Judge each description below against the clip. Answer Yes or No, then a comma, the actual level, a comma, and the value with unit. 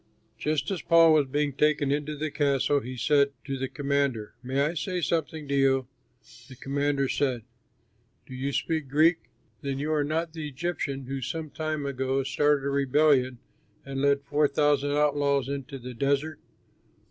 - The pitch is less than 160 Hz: Yes, medium, 140 Hz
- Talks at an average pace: Yes, average, 170 wpm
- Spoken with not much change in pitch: Yes, narrow, 1.9 semitones